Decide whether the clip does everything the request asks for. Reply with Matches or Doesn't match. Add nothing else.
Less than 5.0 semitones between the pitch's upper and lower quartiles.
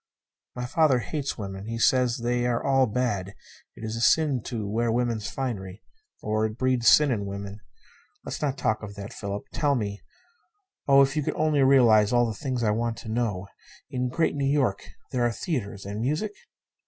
Matches